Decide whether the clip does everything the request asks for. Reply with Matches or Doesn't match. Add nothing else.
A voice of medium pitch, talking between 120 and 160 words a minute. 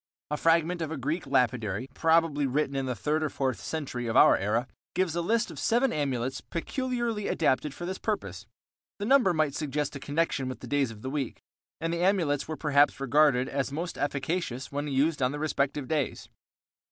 Doesn't match